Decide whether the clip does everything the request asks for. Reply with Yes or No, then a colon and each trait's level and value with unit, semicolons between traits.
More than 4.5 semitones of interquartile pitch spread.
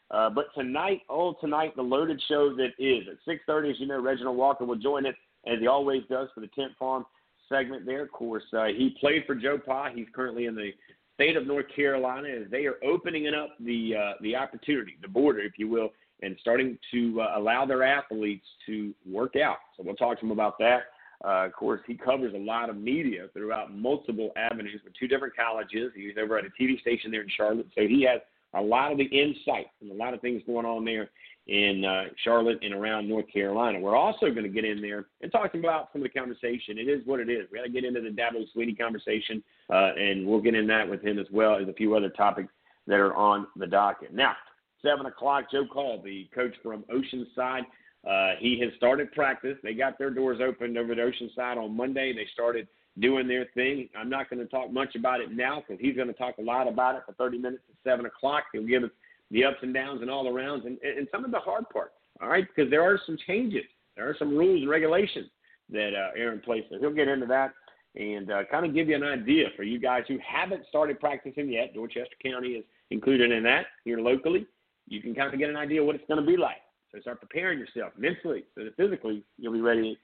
No: average, 3.8 semitones